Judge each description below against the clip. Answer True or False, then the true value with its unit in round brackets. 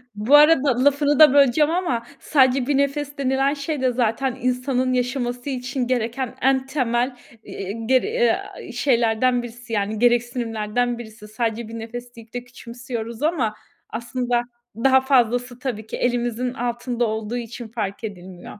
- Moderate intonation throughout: False (2.3 semitones)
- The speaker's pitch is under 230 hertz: False (245 Hz)